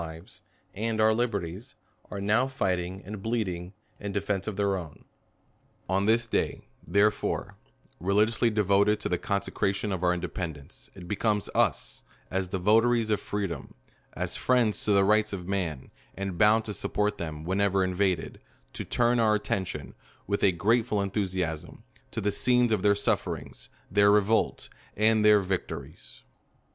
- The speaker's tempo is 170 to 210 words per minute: No, average, 155 wpm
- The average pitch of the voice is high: No, low, 100 Hz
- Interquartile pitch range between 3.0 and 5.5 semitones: No, narrow, 2.6 semitones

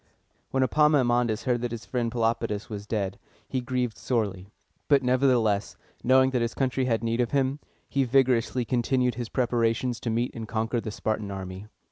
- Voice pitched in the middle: No, low, 120 Hz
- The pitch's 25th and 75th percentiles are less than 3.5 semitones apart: Yes, narrow, 2.5 semitones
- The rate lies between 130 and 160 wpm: No, average, 170 wpm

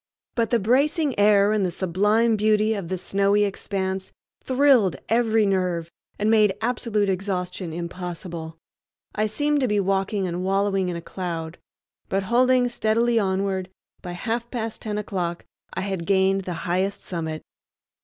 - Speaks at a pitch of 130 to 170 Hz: No, high, 195 Hz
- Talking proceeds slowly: No, average, 150 wpm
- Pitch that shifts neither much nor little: Yes, average, 3.2 semitones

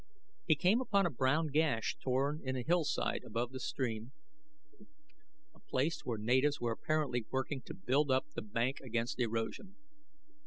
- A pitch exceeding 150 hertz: No, low, 130 Hz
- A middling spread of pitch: Yes, average, 4.0 semitones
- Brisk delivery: No, average, 155 wpm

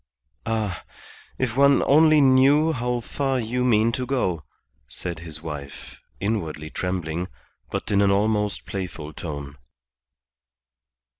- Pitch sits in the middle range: No, low, 105 Hz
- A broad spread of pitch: Yes, wide, 7.4 semitones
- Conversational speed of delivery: No, slow, 120 wpm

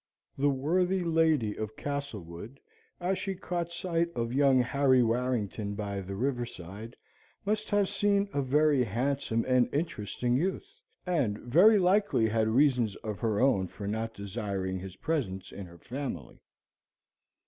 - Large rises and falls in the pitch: Yes, wide, 7.2 semitones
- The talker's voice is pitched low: Yes, low, 125 Hz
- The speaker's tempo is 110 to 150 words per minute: Yes, average, 145 wpm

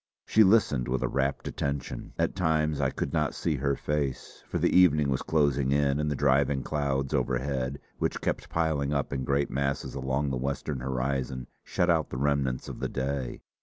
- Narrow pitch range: Yes, narrow, 1.9 semitones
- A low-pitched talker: Yes, very low, 70 Hz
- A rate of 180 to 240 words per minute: Yes, average, 190 wpm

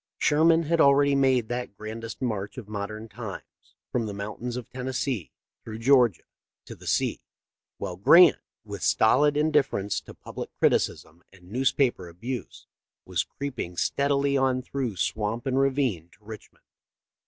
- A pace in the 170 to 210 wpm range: No, average, 145 wpm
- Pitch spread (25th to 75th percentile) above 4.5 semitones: Yes, average, 5.0 semitones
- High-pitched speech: No, low, 120 Hz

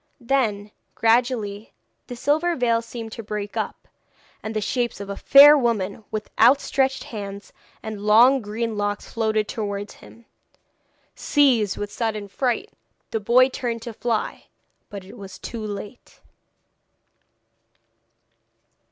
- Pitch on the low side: No, high, 225 Hz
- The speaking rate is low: Yes, slow, 125 wpm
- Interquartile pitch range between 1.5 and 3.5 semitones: Yes, average, 2.9 semitones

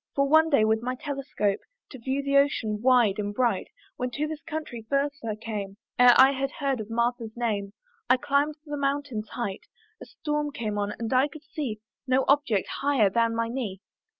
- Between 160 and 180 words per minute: No, average, 195 wpm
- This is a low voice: No, very high, 250 Hz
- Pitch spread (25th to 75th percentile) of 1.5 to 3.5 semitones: No, average, 4.3 semitones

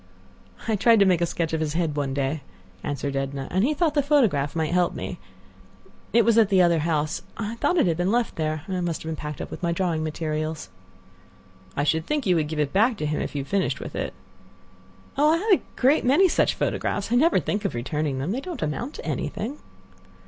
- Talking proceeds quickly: Yes, fast, 235 wpm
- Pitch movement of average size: No, wide, 7.2 semitones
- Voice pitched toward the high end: No, medium, 170 Hz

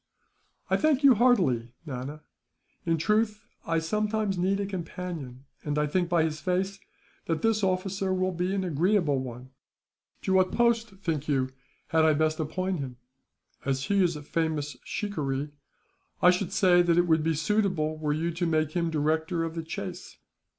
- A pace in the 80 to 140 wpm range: No, average, 170 wpm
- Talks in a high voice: No, medium, 170 Hz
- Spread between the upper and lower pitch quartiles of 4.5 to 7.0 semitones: No, average, 3.9 semitones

